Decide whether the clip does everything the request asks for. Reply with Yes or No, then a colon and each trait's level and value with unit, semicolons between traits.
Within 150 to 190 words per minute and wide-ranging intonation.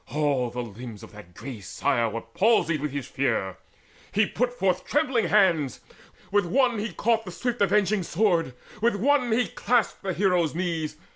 Yes: average, 170 wpm; wide, 8.4 semitones